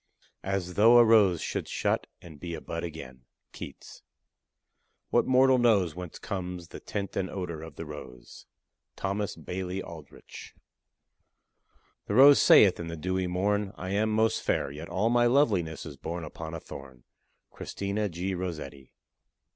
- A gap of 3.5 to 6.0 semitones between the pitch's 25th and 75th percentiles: Yes, average, 4.2 semitones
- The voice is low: Yes, very low, 90 Hz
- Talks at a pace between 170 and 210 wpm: No, average, 155 wpm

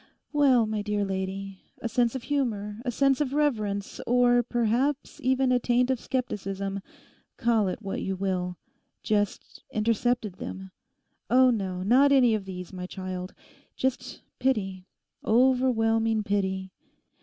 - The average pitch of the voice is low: No, high, 220 Hz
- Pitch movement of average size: Yes, average, 4.5 semitones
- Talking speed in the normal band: No, slow, 130 wpm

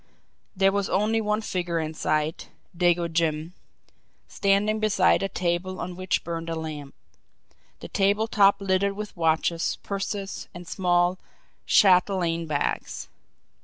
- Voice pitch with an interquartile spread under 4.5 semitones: Yes, average, 3.0 semitones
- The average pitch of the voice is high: No, medium, 180 Hz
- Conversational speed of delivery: No, slow, 130 wpm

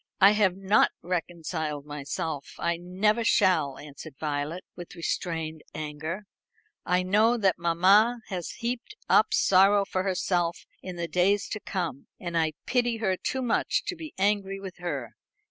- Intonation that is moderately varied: Yes, average, 3.8 semitones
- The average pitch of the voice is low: No, medium, 180 Hz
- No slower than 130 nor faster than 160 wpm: Yes, average, 150 wpm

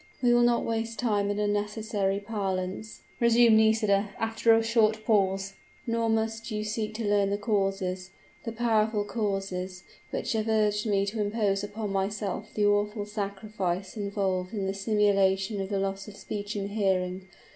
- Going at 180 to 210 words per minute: No, average, 155 wpm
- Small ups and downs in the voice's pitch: Yes, narrow, 2.0 semitones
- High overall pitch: Yes, high, 205 Hz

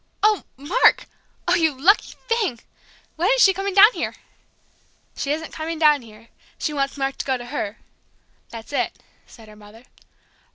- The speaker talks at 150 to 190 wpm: Yes, average, 165 wpm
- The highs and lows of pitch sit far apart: Yes, wide, 7.5 semitones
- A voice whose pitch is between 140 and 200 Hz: No, very high, 295 Hz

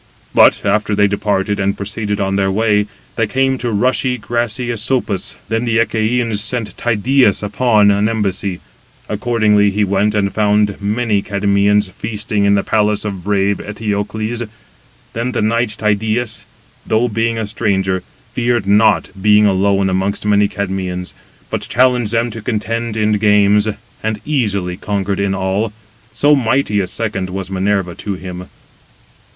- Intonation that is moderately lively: No, narrow, 2.2 semitones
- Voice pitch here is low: Yes, low, 105 Hz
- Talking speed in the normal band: Yes, average, 150 wpm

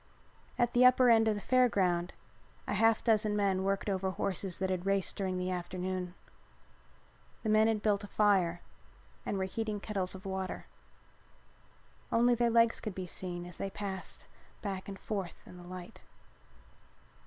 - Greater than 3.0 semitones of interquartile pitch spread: No, average, 2.7 semitones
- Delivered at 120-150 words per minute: No, average, 165 wpm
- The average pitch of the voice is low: No, high, 195 Hz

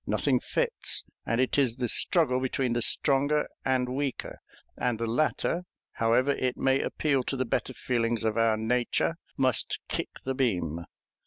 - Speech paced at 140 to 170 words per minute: Yes, average, 160 wpm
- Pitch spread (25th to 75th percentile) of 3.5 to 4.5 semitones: No, average, 2.8 semitones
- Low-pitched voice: Yes, low, 130 Hz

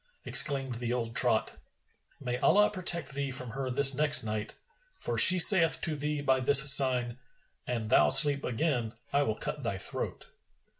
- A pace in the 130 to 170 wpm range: Yes, average, 165 wpm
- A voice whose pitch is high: No, low, 135 Hz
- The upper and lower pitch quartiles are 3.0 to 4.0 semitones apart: Yes, average, 3.5 semitones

